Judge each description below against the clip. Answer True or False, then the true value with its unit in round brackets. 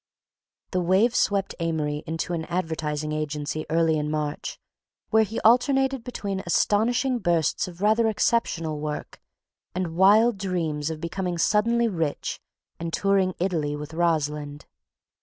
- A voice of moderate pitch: True (175 Hz)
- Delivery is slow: True (130 wpm)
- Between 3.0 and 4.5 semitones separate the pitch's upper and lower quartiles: False (5.0 semitones)